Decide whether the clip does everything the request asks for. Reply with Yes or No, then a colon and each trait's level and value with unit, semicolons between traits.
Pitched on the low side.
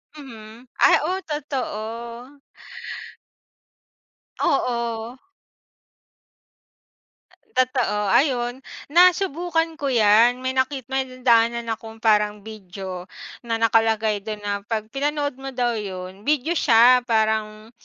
No: high, 235 Hz